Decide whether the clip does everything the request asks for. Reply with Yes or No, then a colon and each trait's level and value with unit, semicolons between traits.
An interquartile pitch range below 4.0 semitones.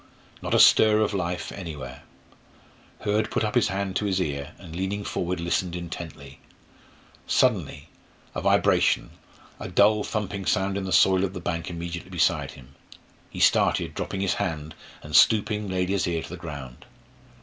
Yes: average, 3.2 semitones